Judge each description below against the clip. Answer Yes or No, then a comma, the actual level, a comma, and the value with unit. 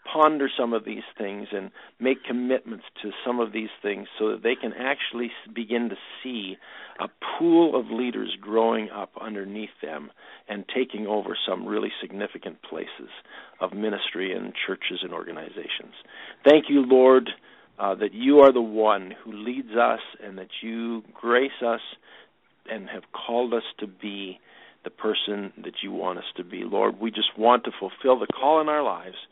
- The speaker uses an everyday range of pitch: Yes, average, 3.4 semitones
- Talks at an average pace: Yes, average, 170 wpm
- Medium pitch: No, low, 115 Hz